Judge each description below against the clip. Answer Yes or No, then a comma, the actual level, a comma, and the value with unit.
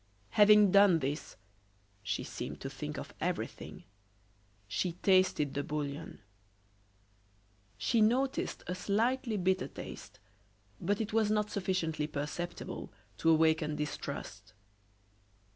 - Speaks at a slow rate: Yes, slow, 110 wpm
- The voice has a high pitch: No, medium, 180 Hz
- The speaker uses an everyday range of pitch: No, wide, 5.7 semitones